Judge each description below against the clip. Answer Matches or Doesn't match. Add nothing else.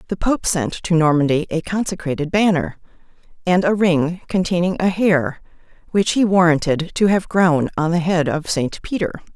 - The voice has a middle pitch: Matches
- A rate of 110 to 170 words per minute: Matches